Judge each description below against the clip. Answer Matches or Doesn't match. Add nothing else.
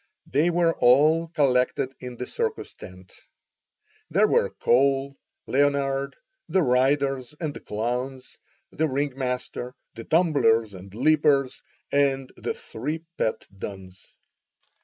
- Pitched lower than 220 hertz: Matches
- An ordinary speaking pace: Doesn't match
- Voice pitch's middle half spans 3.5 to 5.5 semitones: Doesn't match